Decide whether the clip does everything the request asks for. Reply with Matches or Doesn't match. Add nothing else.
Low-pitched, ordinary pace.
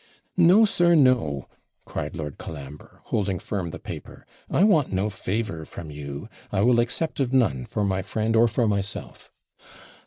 Matches